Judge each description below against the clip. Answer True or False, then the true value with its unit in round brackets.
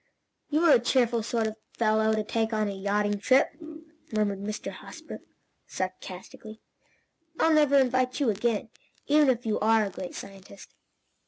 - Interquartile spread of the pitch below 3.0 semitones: False (3.4 semitones)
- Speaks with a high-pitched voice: True (220 Hz)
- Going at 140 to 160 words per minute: True (150 wpm)